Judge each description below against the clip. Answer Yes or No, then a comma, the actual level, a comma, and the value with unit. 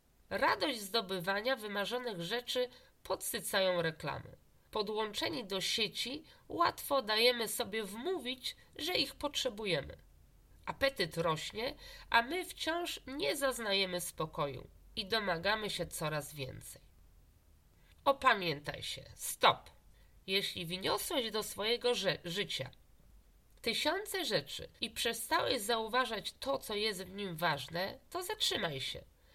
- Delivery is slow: Yes, slow, 105 wpm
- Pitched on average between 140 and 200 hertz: No, high, 215 Hz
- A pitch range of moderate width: No, wide, 6.5 semitones